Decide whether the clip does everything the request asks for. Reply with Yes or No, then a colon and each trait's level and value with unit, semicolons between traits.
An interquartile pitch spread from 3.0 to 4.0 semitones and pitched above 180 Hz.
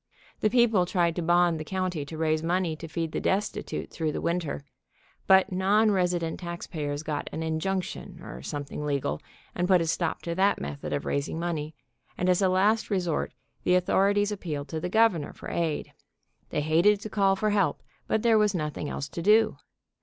No: average, 3.5 semitones; medium, 175 Hz